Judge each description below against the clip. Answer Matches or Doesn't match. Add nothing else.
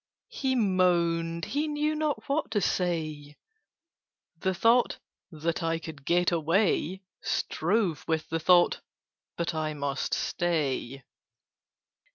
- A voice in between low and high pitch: Matches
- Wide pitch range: Doesn't match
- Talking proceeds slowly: Matches